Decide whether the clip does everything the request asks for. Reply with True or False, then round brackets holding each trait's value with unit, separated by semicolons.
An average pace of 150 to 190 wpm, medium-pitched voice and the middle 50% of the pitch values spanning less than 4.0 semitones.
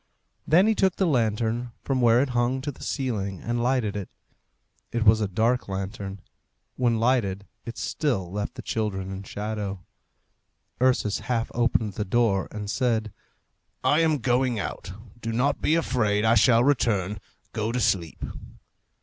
False (160 wpm; 115 Hz; 3.6 semitones)